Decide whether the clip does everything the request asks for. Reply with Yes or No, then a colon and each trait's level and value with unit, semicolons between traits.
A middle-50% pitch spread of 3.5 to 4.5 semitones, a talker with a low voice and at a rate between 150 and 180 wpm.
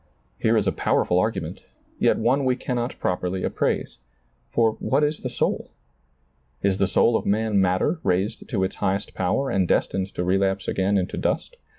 Yes: average, 3.9 semitones; low, 100 Hz; average, 175 wpm